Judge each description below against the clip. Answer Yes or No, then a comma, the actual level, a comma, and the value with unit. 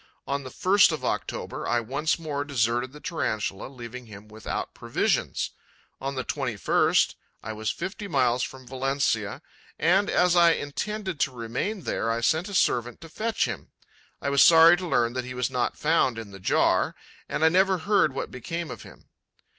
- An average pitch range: No, wide, 5.8 semitones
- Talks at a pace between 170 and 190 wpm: Yes, average, 180 wpm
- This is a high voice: No, medium, 140 Hz